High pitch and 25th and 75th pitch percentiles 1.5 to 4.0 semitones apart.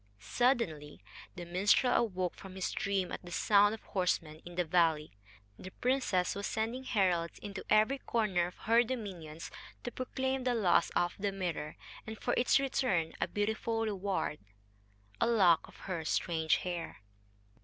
No: high, 195 Hz; average, 4.7 semitones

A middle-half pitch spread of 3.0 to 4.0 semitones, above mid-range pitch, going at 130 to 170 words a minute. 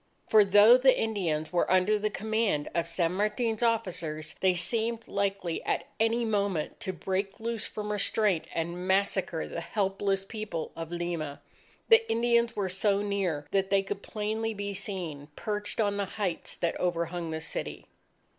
Yes: average, 3.7 semitones; high, 200 Hz; average, 160 wpm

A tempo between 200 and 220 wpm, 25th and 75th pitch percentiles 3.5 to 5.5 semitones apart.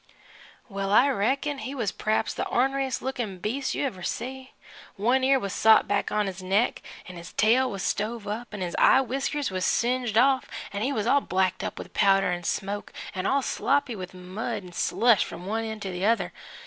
Yes: fast, 205 wpm; average, 4.9 semitones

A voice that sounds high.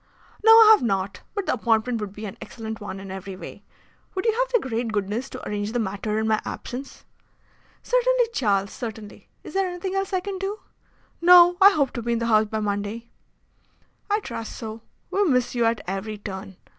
Yes: high, 230 Hz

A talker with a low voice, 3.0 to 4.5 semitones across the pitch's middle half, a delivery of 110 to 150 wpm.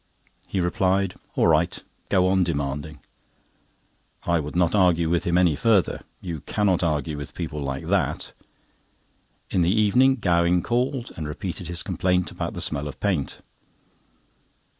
Yes: very low, 90 Hz; average, 3.6 semitones; average, 145 wpm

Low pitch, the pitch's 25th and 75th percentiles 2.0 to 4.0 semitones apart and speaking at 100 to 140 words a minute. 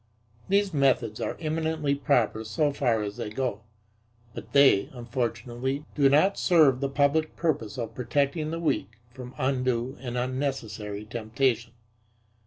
Yes: low, 130 Hz; average, 3.7 semitones; slow, 135 wpm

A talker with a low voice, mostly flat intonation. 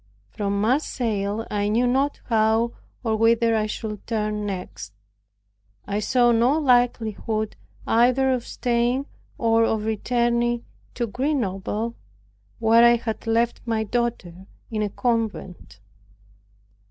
No: high, 225 Hz; narrow, 2.1 semitones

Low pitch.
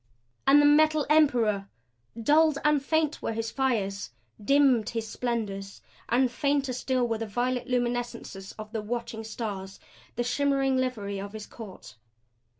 No: high, 240 Hz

